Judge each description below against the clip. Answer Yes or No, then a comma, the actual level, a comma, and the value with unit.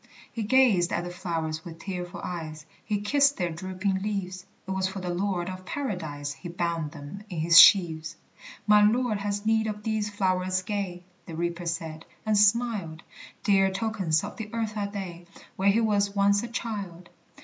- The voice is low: No, high, 190 Hz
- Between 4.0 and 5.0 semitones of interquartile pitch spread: No, average, 3.4 semitones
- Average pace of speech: Yes, average, 180 wpm